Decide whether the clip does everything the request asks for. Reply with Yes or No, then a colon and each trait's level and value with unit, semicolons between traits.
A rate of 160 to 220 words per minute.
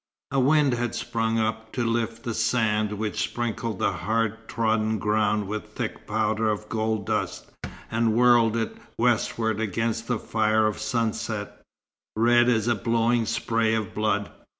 No: average, 150 wpm